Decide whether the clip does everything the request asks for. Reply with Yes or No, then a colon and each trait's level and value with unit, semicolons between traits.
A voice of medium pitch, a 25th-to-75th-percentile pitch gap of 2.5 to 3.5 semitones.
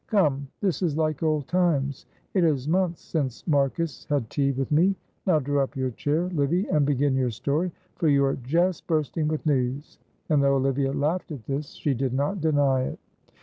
Yes: medium, 145 Hz; average, 3.0 semitones